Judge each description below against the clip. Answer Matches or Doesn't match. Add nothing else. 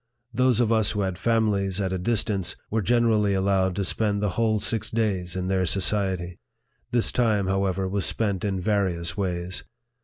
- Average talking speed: Matches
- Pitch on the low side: Matches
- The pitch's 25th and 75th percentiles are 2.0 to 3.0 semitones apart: Matches